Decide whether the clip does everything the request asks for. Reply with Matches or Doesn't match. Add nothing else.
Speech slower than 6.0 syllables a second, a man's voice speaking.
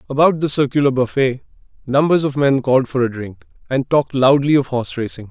Matches